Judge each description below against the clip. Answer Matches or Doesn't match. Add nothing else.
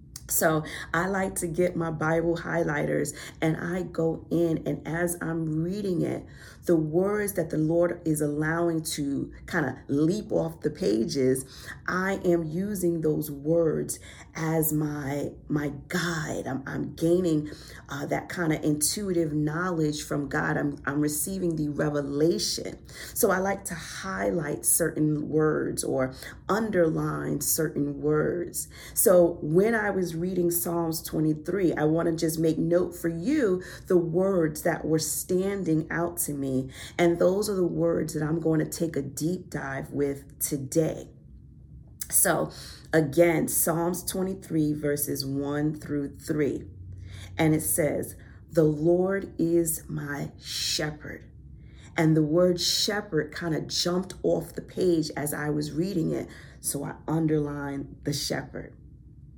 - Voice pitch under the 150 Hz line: Doesn't match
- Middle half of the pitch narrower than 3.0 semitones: Matches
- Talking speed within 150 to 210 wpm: Doesn't match